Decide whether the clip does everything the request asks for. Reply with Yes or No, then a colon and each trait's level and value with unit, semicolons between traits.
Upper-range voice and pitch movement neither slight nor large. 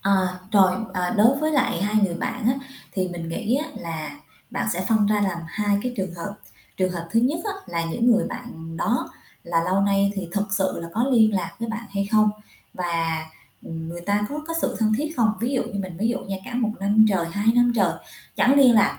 Yes: high, 205 Hz; average, 4.5 semitones